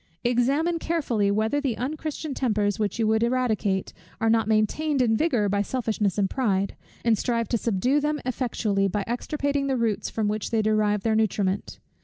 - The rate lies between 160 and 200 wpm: Yes, average, 175 wpm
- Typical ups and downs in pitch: Yes, average, 3.9 semitones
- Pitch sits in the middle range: No, high, 225 Hz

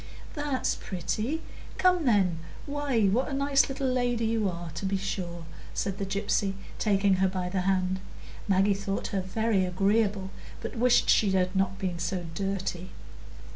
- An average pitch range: Yes, average, 3.6 semitones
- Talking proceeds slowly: No, average, 160 wpm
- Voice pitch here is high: Yes, high, 195 Hz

